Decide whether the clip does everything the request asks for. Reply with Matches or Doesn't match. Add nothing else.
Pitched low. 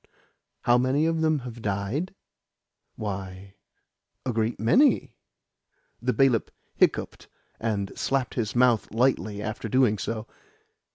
Matches